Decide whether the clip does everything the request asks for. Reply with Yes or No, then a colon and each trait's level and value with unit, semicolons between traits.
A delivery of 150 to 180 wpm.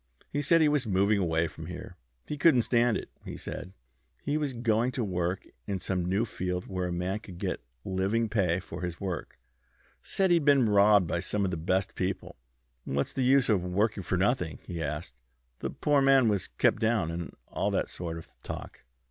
No: average, 200 wpm